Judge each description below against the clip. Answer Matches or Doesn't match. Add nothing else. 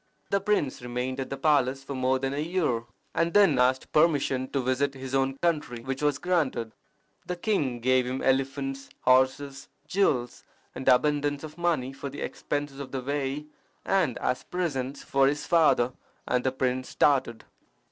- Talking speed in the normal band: Matches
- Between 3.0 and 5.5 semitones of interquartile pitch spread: Doesn't match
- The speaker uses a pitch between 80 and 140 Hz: Matches